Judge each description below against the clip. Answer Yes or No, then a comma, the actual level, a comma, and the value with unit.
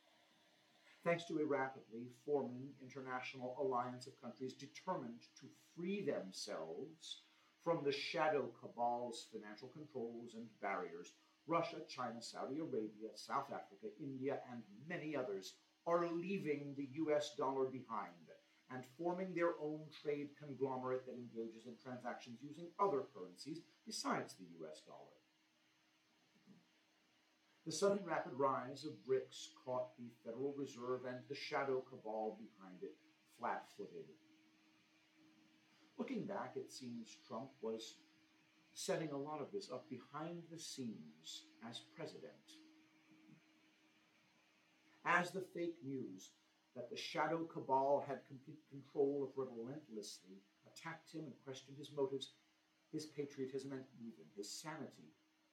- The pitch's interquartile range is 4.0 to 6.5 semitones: Yes, average, 4.4 semitones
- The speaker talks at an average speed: No, slow, 120 wpm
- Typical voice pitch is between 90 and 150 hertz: Yes, medium, 140 Hz